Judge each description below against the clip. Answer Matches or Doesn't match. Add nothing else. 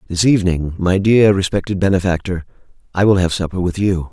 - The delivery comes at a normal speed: Matches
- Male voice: Matches